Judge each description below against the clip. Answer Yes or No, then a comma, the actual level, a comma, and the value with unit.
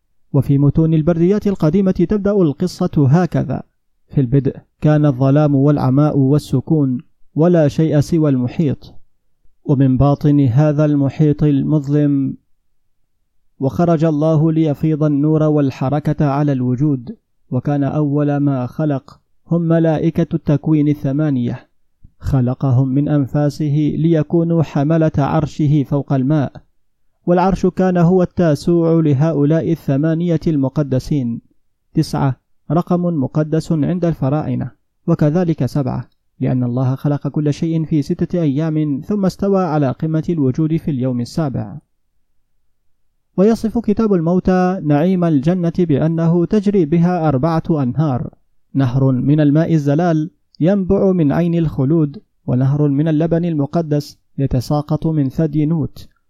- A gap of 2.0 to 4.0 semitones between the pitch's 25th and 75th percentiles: Yes, average, 2.9 semitones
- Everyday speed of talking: Yes, average, 110 wpm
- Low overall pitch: No, medium, 150 Hz